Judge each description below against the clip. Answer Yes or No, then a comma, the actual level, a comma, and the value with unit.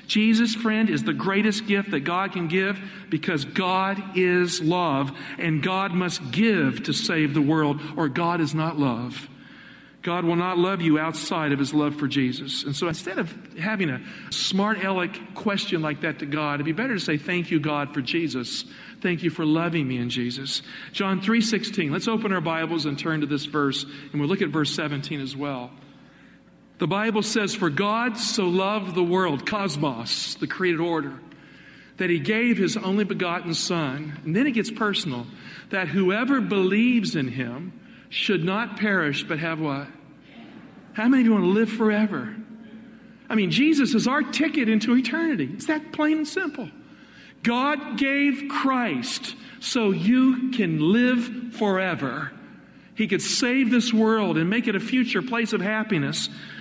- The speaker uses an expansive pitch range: Yes, wide, 6.3 semitones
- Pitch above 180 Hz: Yes, high, 190 Hz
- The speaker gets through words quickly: No, average, 175 wpm